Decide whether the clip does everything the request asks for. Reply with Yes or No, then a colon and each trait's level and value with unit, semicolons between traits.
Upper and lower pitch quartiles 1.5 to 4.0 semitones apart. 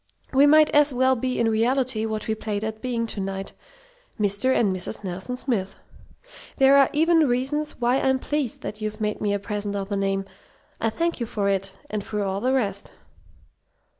No: average, 4.4 semitones